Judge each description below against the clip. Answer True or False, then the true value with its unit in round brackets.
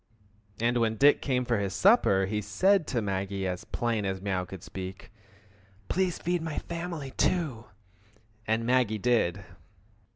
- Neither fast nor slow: True (150 wpm)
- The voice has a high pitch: False (115 Hz)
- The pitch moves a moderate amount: False (7.0 semitones)